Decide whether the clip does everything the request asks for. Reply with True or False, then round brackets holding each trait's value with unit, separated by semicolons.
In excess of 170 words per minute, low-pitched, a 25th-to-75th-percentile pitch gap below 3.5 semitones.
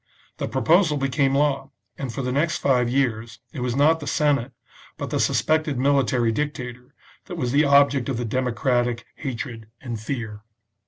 False (165 wpm; 130 Hz; 2.8 semitones)